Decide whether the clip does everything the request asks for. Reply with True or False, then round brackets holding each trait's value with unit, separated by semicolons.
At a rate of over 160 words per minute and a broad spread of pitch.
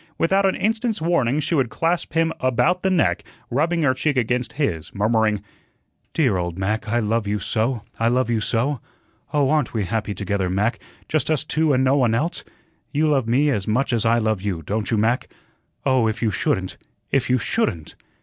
True (195 wpm; 5.7 semitones)